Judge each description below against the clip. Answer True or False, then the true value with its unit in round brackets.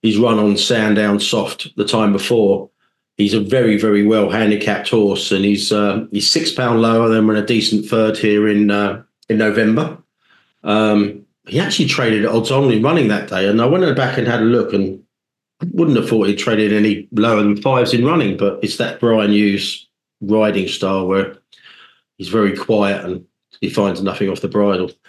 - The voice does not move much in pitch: True (2.0 semitones)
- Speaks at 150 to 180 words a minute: False (195 wpm)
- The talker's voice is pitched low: True (105 Hz)